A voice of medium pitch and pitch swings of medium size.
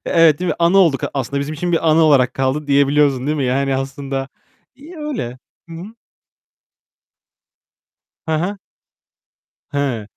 Yes: medium, 145 Hz; average, 3.7 semitones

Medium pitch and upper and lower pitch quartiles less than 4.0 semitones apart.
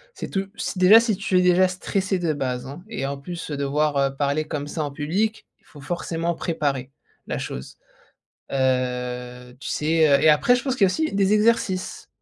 No: medium, 155 Hz; average, 5.3 semitones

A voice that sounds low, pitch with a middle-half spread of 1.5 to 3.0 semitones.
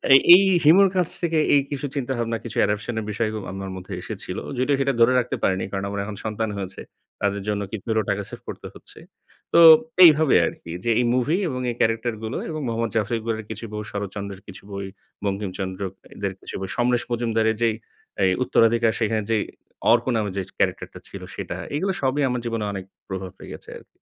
No: low, 110 Hz; average, 3.5 semitones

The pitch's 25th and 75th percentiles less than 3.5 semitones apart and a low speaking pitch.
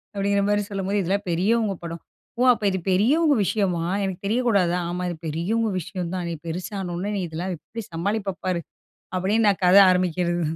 No: average, 2.9 semitones; high, 190 Hz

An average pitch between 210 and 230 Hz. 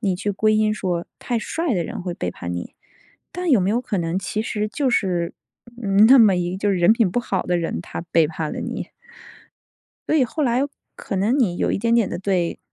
No: high, 200 Hz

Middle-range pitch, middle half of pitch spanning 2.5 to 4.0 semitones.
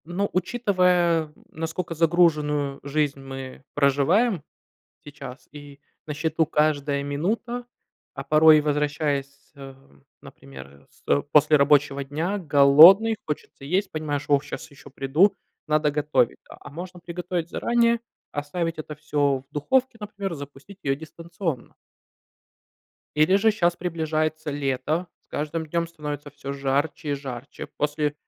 Yes: medium, 150 Hz; average, 3.3 semitones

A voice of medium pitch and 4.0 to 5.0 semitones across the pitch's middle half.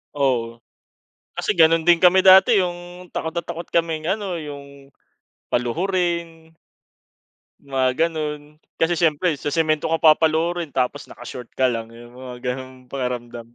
Yes: medium, 155 Hz; average, 4.7 semitones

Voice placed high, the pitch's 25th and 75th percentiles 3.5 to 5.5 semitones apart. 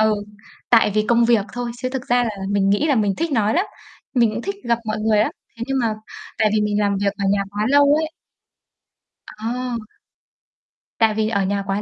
No: high, 220 Hz; average, 2.8 semitones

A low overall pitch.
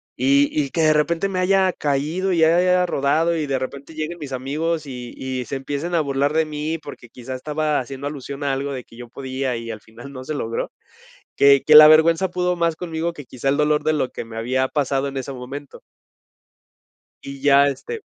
No: medium, 145 Hz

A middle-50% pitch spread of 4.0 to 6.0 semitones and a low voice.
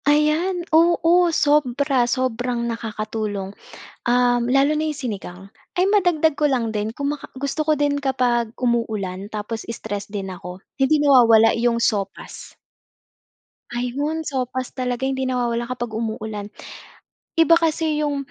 No: average, 4.6 semitones; very high, 250 Hz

